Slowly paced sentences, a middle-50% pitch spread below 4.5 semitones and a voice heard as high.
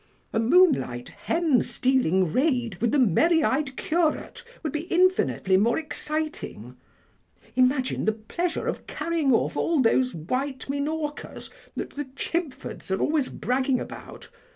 No: slow, 130 wpm; average, 4.8 semitones; very high, 270 Hz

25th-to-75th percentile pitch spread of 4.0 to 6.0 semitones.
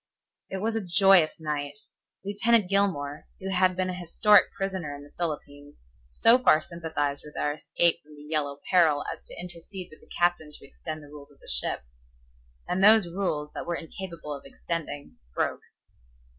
Yes: average, 4.3 semitones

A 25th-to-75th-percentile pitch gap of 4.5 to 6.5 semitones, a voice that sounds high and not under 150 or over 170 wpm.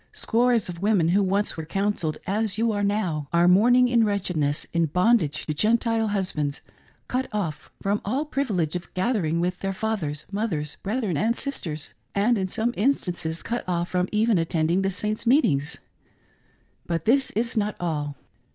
Yes: average, 4.9 semitones; high, 195 Hz; average, 165 wpm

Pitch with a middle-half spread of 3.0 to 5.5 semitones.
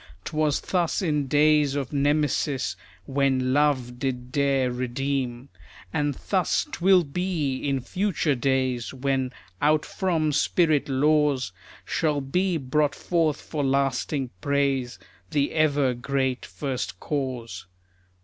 No: narrow, 2.6 semitones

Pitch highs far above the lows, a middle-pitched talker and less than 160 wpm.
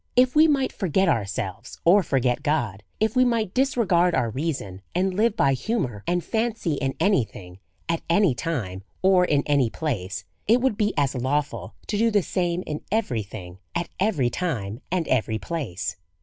No: wide, 9.0 semitones; medium, 165 Hz; average, 180 wpm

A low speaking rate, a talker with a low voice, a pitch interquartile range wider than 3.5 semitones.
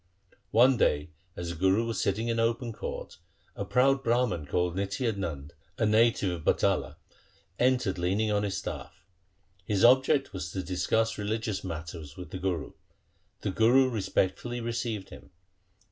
No: average, 150 wpm; low, 105 Hz; average, 4.3 semitones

